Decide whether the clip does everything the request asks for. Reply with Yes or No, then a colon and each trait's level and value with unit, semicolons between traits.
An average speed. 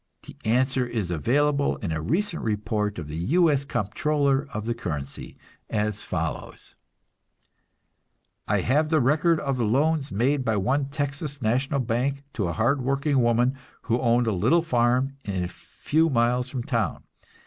Yes: average, 160 wpm